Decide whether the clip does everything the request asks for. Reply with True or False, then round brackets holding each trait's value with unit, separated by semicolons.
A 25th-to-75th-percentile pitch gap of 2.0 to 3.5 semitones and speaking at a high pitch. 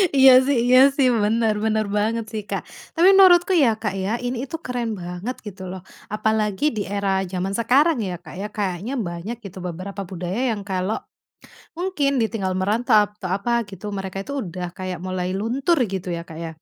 False (4.6 semitones; 210 Hz)